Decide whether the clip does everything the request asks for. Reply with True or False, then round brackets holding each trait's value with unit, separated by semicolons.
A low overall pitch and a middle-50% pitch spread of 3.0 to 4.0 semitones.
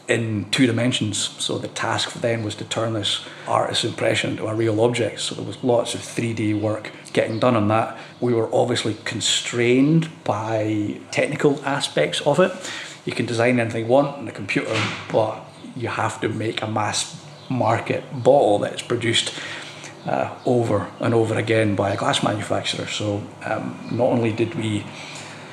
False (115 Hz; 2.6 semitones)